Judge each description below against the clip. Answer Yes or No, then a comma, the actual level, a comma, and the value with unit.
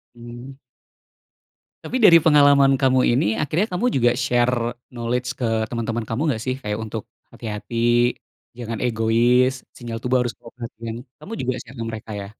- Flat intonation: Yes, narrow, 2.2 semitones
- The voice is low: Yes, low, 120 Hz